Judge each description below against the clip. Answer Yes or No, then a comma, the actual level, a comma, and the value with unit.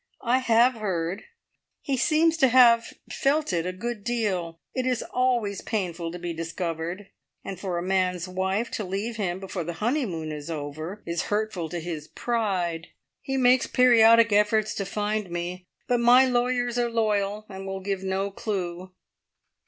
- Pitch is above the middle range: Yes, high, 200 Hz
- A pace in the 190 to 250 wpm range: No, average, 165 wpm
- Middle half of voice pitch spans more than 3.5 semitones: Yes, average, 5.0 semitones